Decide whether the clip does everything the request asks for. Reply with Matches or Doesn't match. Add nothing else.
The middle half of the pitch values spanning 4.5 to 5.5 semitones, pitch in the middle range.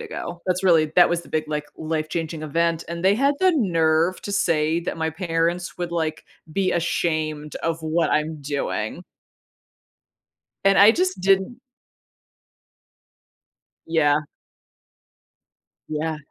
Doesn't match